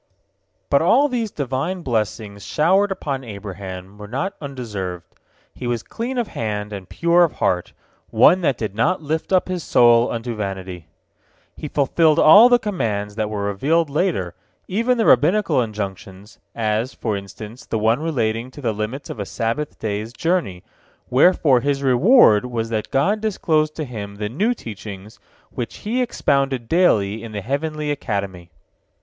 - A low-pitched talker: Yes, low, 125 Hz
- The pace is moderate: Yes, average, 160 wpm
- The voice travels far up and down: Yes, wide, 7.4 semitones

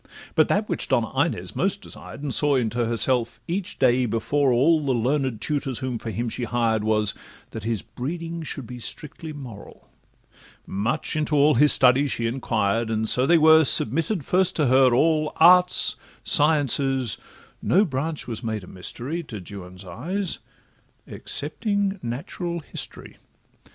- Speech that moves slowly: No, average, 155 wpm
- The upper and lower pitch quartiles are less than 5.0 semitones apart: No, average, 5.3 semitones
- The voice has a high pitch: No, low, 130 Hz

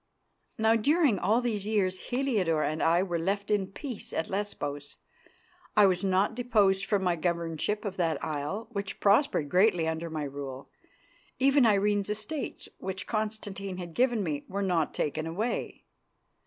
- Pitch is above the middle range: Yes, high, 195 Hz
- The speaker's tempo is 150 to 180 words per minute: Yes, average, 155 wpm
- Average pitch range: Yes, average, 4.4 semitones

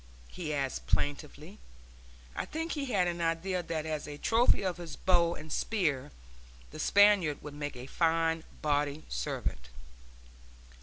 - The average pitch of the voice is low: No, medium, 165 Hz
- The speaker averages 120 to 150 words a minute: Yes, average, 145 wpm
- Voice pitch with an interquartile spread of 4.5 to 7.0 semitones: No, average, 3.7 semitones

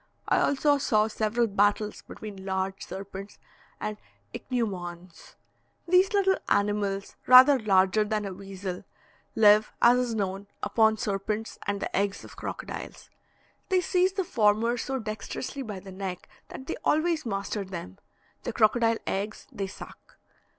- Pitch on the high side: Yes, high, 210 Hz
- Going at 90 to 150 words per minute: Yes, average, 140 wpm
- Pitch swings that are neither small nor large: Yes, average, 3.5 semitones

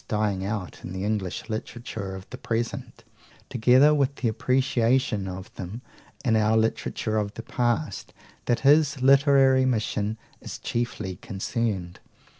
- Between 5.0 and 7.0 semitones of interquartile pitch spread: No, average, 3.9 semitones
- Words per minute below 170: Yes, slow, 135 wpm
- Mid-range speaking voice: No, low, 115 Hz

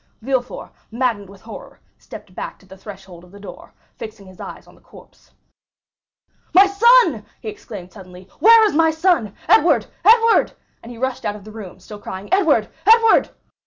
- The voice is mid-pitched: No, high, 225 Hz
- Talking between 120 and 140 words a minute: No, average, 170 wpm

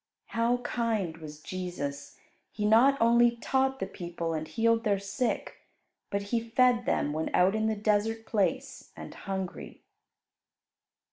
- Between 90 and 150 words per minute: Yes, average, 140 wpm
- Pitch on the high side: Yes, high, 215 Hz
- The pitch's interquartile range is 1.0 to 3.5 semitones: No, average, 4.5 semitones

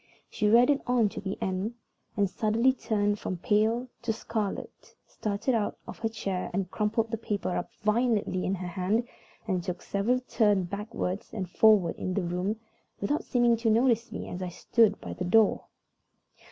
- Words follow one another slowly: No, average, 170 wpm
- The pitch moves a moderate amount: Yes, average, 3.3 semitones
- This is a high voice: Yes, high, 210 Hz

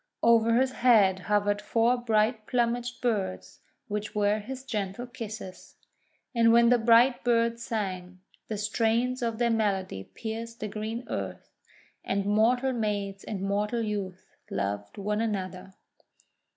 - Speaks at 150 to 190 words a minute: No, slow, 135 wpm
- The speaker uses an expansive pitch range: No, average, 2.7 semitones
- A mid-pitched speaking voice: No, high, 220 Hz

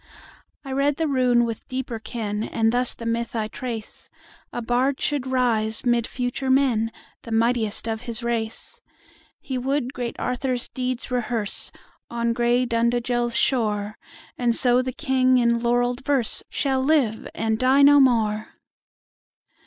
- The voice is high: Yes, high, 240 Hz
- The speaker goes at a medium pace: No, slow, 125 wpm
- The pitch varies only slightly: Yes, narrow, 2.0 semitones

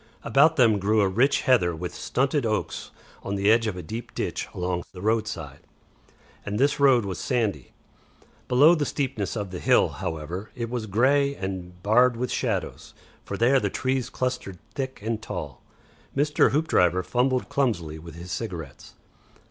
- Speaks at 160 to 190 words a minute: Yes, average, 165 wpm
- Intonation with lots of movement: Yes, wide, 5.9 semitones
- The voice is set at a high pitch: No, low, 110 Hz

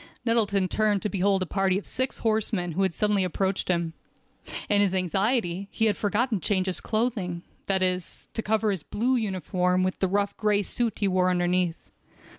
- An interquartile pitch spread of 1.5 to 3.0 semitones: Yes, average, 2.7 semitones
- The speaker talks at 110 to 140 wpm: No, average, 185 wpm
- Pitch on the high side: Yes, high, 195 Hz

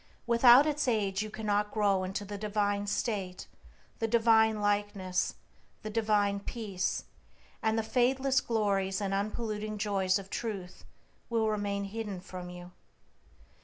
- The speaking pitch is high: Yes, high, 210 Hz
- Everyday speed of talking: No, slow, 130 wpm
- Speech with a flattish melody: Yes, narrow, 2.0 semitones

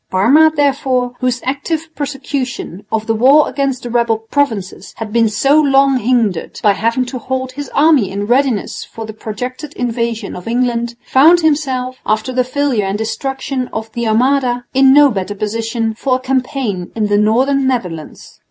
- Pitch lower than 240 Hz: No, very high, 250 Hz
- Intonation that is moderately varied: Yes, average, 3.5 semitones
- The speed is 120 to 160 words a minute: No, average, 170 wpm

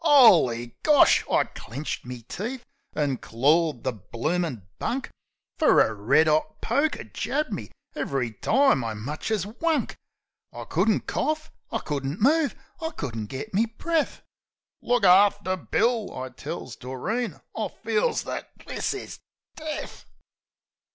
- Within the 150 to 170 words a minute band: No, slow, 135 wpm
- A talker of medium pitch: Yes, medium, 180 Hz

